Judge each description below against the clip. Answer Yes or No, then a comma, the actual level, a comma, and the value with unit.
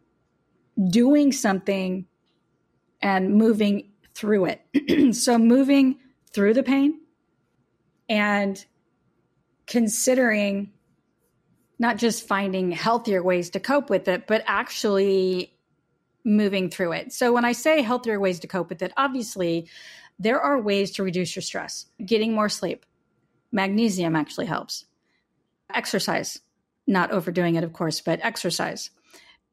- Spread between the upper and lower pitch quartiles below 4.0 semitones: No, average, 4.4 semitones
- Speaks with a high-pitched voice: Yes, high, 205 Hz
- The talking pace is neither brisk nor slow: No, slow, 120 wpm